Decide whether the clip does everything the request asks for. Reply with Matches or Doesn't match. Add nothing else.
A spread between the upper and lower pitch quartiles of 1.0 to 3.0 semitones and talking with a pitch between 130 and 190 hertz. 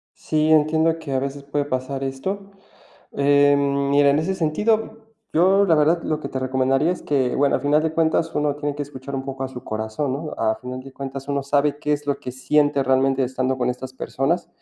Matches